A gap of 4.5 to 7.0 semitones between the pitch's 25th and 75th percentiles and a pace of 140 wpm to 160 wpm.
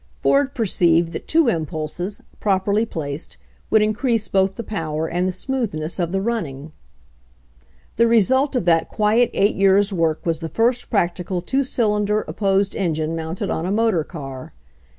Yes: average, 5.1 semitones; average, 155 wpm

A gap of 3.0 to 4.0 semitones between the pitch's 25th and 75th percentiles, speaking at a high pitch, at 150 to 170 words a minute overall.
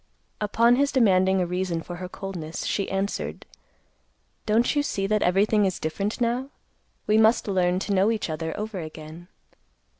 Yes: average, 3.5 semitones; high, 195 Hz; average, 160 wpm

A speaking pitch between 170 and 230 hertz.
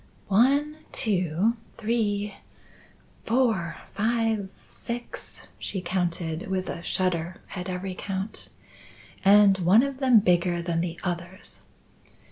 Yes: high, 190 Hz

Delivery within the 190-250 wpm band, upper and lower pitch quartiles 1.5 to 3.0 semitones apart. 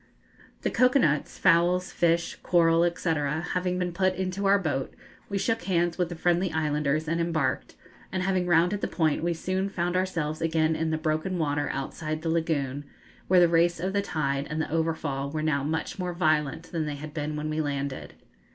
Yes: average, 195 wpm; average, 2.7 semitones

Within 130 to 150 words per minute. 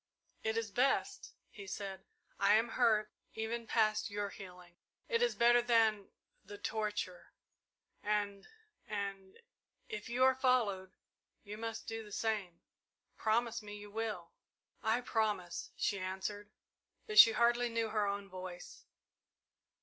Yes: slow, 135 wpm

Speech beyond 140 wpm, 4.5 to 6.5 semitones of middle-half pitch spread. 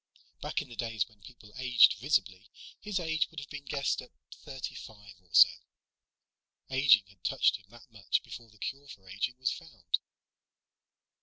Yes: average, 170 wpm; average, 5.1 semitones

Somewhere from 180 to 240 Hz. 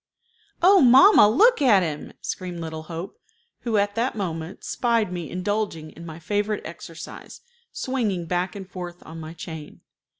Yes: medium, 185 Hz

